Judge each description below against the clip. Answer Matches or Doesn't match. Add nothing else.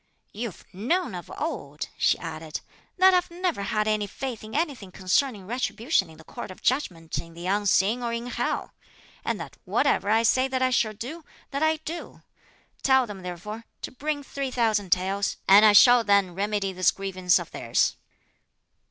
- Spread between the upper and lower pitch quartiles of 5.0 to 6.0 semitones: Matches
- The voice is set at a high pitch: Matches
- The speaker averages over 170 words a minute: Matches